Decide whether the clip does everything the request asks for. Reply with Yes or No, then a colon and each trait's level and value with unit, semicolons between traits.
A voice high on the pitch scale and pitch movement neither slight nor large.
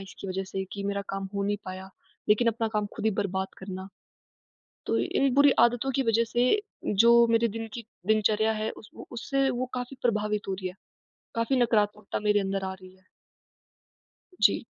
Yes: high, 210 Hz; average, 3.1 semitones